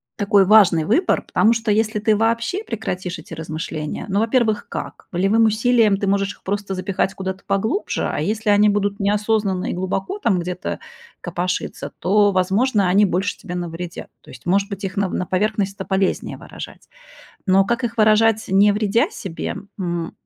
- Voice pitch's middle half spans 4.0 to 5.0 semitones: No, average, 2.7 semitones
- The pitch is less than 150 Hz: No, high, 200 Hz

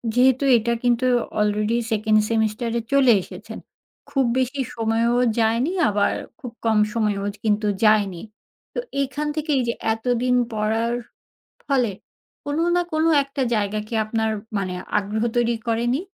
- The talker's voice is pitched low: No, high, 230 Hz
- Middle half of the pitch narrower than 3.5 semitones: Yes, average, 2.9 semitones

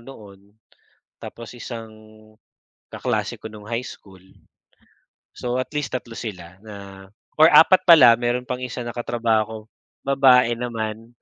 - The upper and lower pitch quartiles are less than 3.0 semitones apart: Yes, narrow, 2.4 semitones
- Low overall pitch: Yes, low, 115 Hz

